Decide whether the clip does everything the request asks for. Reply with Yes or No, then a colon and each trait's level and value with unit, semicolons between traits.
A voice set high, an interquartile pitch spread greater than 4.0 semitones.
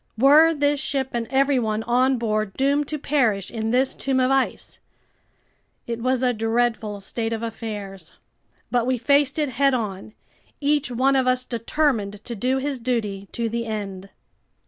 No: high, 245 Hz; average, 3.5 semitones